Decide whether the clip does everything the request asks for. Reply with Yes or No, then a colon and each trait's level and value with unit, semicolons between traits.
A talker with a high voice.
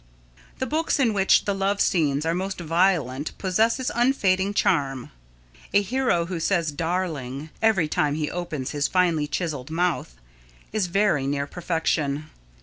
No: medium, 170 Hz